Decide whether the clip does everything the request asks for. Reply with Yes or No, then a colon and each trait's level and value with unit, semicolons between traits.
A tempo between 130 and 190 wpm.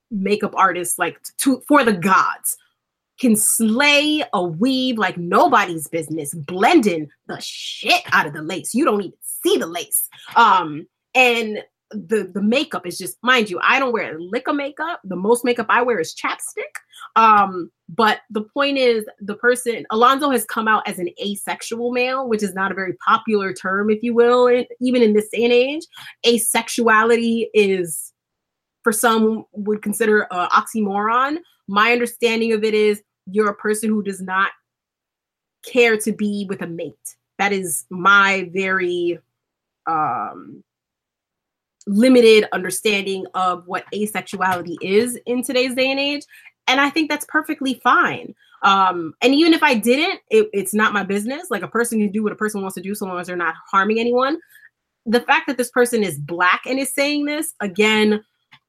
Yes: average, 175 wpm